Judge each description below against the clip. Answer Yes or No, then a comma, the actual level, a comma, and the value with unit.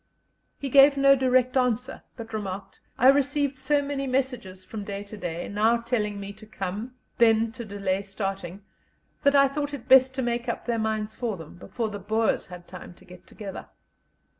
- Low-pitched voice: No, high, 225 Hz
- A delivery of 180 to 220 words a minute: Yes, average, 190 wpm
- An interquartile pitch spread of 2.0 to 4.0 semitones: No, average, 4.7 semitones